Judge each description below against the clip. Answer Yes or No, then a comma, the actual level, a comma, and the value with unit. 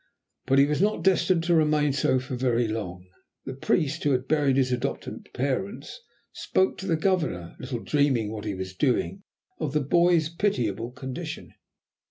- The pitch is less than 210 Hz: Yes, low, 135 Hz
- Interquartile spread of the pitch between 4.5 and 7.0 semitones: Yes, average, 5.0 semitones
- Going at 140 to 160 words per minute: No, average, 170 wpm